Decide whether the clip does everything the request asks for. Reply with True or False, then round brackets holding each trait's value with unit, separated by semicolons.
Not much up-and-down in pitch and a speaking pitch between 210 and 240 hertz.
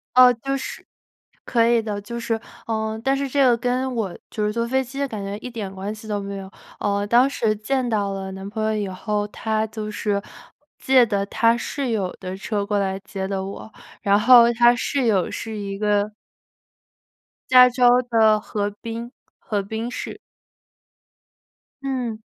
False (3.1 semitones; 220 Hz)